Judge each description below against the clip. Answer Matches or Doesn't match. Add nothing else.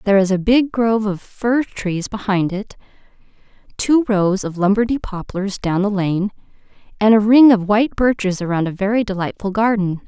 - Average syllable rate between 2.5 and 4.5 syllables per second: Doesn't match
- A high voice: Matches